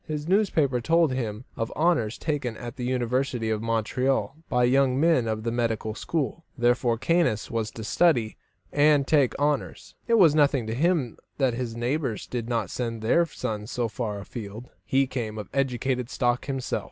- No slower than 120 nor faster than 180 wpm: Yes, average, 175 wpm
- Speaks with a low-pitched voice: Yes, low, 125 Hz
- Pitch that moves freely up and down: No, average, 4.0 semitones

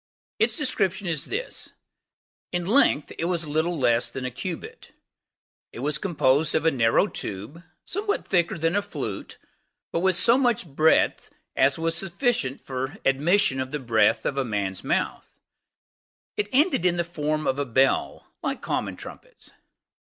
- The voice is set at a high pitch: No, medium, 160 Hz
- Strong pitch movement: Yes, wide, 5.9 semitones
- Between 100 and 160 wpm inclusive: Yes, average, 155 wpm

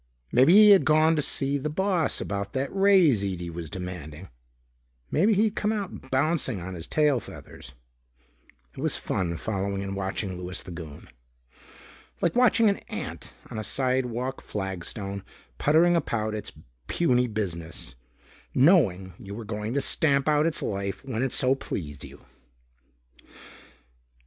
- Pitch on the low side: Yes, low, 120 Hz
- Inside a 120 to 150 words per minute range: Yes, average, 145 wpm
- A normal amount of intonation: No, wide, 8.1 semitones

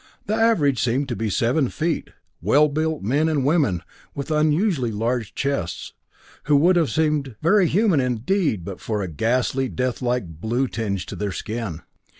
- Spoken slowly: No, average, 165 wpm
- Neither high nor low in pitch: No, low, 130 Hz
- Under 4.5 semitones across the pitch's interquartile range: No, wide, 5.6 semitones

